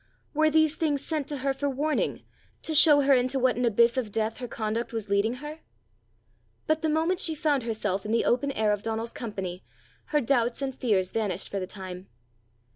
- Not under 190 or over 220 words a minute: Yes, average, 200 wpm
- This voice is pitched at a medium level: No, high, 245 Hz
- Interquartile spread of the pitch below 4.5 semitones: No, average, 5.2 semitones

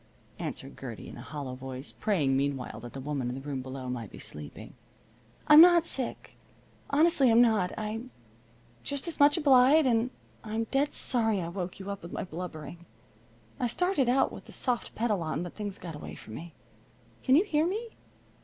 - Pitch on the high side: Yes, high, 205 Hz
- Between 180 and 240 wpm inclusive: Yes, average, 190 wpm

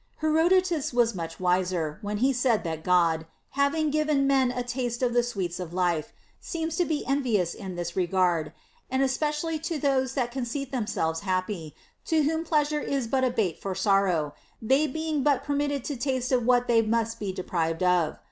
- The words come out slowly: No, average, 195 wpm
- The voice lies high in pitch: Yes, high, 240 Hz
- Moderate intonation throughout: No, wide, 7.4 semitones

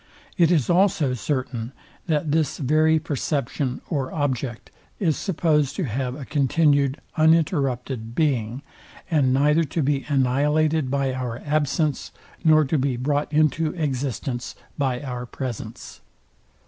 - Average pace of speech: No, slow, 125 wpm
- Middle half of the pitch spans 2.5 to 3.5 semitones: Yes, average, 3.2 semitones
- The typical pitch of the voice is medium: Yes, medium, 145 Hz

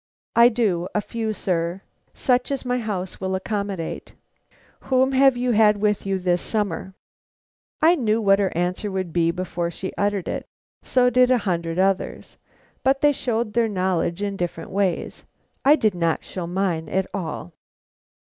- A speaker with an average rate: Yes, average, 165 wpm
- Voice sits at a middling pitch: No, high, 200 Hz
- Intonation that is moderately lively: Yes, average, 4.5 semitones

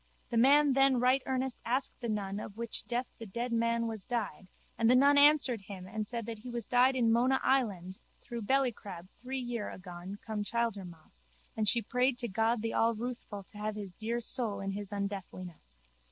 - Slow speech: No, average, 195 wpm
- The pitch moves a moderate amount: Yes, average, 3.6 semitones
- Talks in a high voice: Yes, high, 230 Hz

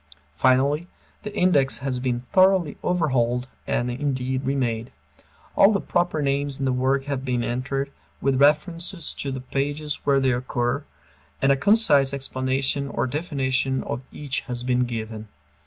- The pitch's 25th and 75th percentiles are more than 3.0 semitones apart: No, narrow, 2.4 semitones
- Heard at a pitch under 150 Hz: Yes, low, 135 Hz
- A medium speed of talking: Yes, average, 150 wpm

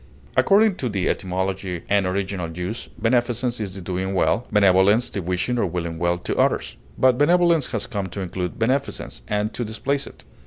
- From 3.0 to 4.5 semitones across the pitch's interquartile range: No, average, 4.9 semitones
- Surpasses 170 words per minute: Yes, average, 180 wpm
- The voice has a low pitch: Yes, low, 100 Hz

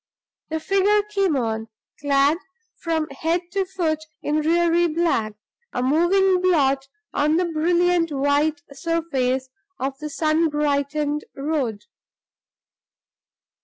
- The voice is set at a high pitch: Yes, very high, 310 Hz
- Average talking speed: No, slow, 110 wpm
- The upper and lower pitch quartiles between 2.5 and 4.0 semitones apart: Yes, average, 3.5 semitones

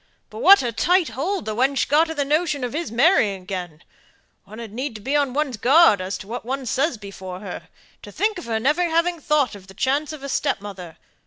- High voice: Yes, very high, 265 Hz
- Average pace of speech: No, fast, 225 wpm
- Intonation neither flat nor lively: No, wide, 6.6 semitones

